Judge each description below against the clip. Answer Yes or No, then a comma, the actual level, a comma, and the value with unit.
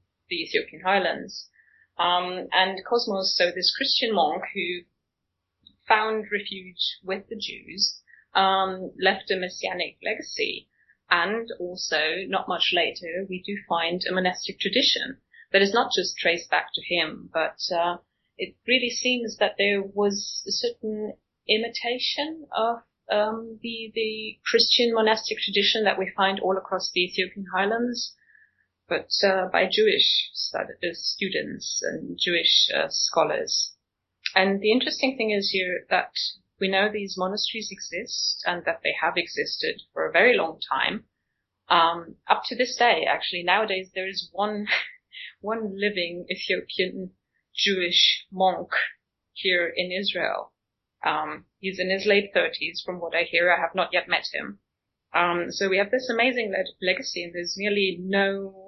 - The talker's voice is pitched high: Yes, high, 195 Hz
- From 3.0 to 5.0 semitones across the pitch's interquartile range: Yes, average, 3.7 semitones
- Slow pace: No, average, 145 wpm